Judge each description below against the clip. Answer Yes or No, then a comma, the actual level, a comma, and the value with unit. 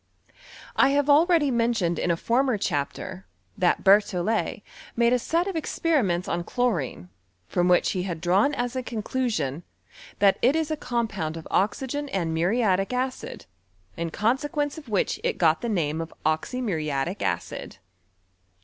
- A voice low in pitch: No, high, 215 Hz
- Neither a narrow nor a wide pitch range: No, wide, 6.9 semitones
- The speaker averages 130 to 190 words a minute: Yes, average, 150 wpm